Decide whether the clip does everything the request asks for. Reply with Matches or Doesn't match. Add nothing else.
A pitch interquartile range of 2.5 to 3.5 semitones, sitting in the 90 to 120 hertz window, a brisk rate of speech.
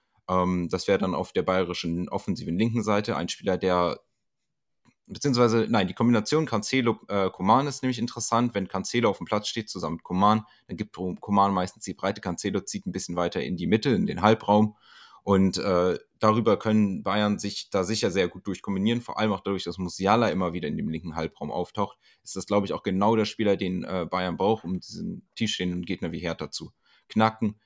Matches